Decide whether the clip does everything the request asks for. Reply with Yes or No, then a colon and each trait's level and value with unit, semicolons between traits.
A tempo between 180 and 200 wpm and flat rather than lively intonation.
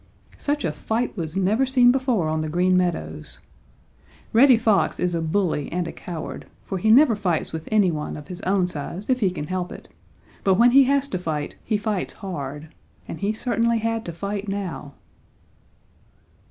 No: average, 185 wpm; average, 5.2 semitones